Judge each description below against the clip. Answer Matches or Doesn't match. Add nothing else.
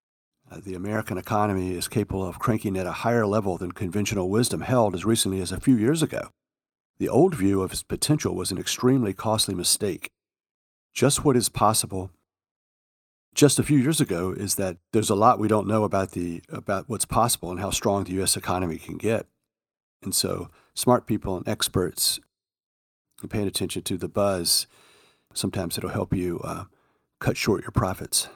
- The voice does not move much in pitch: Doesn't match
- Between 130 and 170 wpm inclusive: Doesn't match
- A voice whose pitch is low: Matches